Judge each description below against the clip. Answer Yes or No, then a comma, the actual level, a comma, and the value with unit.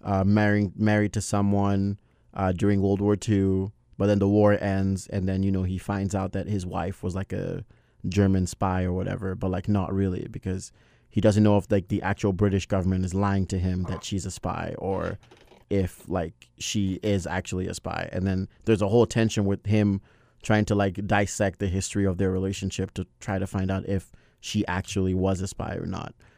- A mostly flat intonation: Yes, narrow, 1.6 semitones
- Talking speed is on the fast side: Yes, fast, 210 wpm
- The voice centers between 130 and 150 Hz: No, low, 100 Hz